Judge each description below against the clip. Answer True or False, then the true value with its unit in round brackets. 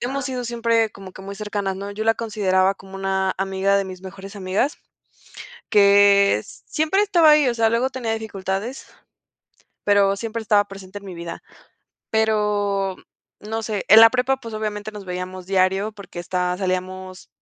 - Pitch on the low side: False (200 Hz)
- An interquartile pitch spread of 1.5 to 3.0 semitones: True (2.7 semitones)